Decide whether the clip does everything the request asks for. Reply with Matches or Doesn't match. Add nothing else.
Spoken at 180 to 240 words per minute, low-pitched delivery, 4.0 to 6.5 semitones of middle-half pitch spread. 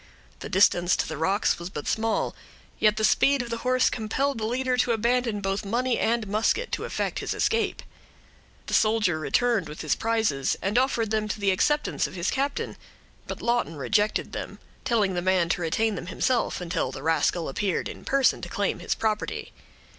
Doesn't match